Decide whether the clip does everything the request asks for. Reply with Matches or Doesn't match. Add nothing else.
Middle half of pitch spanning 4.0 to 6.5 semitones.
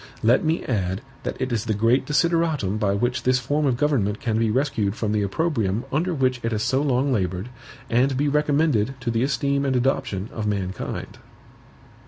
Matches